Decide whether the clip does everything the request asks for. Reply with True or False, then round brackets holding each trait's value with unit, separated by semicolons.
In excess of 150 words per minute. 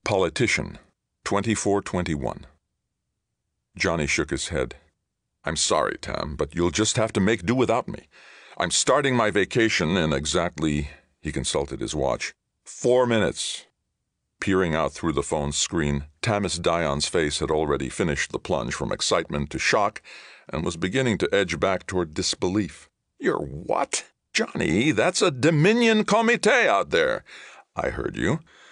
False (140 wpm)